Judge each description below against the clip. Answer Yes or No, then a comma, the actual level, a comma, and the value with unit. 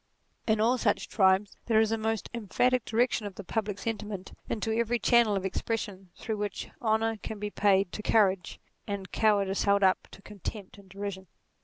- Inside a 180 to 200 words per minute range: Yes, average, 185 wpm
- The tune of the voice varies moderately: No, narrow, 2.2 semitones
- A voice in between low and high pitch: No, high, 210 Hz